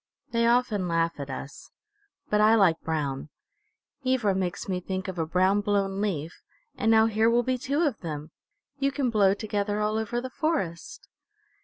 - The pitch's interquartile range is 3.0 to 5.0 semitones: Yes, average, 4.7 semitones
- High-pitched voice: Yes, high, 205 Hz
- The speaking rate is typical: Yes, average, 175 wpm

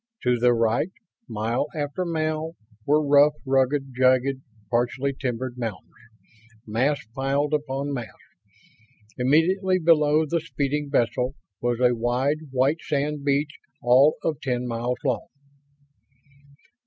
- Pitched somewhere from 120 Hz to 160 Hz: Yes, low, 135 Hz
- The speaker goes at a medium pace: No, slow, 115 wpm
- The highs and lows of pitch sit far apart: No, average, 3.3 semitones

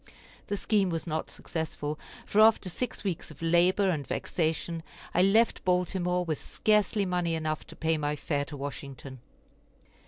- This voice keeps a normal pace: Yes, average, 155 wpm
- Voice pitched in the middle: Yes, medium, 170 Hz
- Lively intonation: No, average, 3.4 semitones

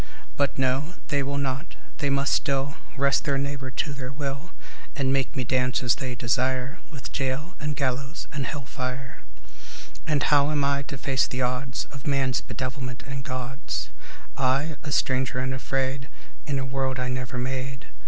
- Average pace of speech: Yes, average, 175 wpm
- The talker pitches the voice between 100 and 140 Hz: Yes, low, 135 Hz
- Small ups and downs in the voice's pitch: Yes, narrow, 1.5 semitones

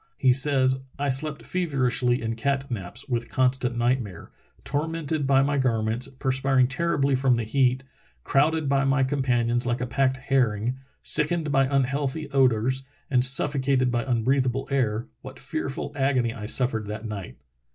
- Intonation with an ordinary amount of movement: No, narrow, 2.2 semitones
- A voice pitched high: No, low, 130 Hz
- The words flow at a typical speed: Yes, average, 150 wpm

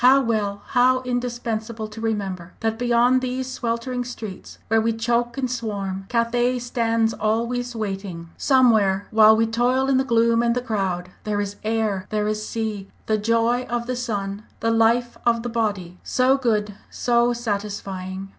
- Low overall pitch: No, high, 225 Hz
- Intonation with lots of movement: No, average, 2.7 semitones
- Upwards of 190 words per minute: No, average, 165 wpm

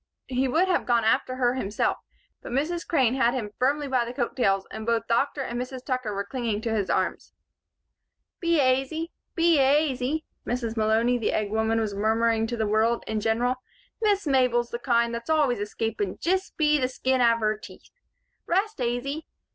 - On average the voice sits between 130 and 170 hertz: No, high, 245 Hz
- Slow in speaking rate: No, average, 185 wpm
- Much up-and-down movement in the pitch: No, average, 3.6 semitones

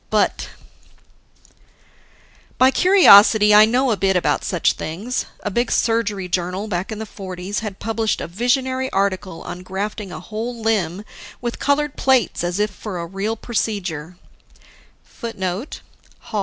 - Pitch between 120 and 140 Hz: No, high, 210 Hz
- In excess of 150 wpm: No, slow, 135 wpm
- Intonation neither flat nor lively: Yes, average, 3.8 semitones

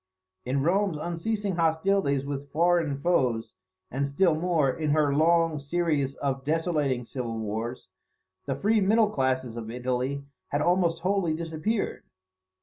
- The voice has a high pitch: No, medium, 155 Hz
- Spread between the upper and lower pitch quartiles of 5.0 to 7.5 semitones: No, average, 4.3 semitones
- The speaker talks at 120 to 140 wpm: Yes, slow, 135 wpm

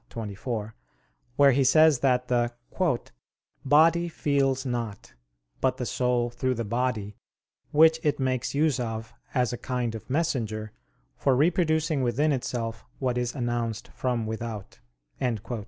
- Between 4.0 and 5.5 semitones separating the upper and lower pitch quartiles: No, average, 3.3 semitones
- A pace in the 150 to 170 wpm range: No, slow, 135 wpm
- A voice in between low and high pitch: No, low, 125 Hz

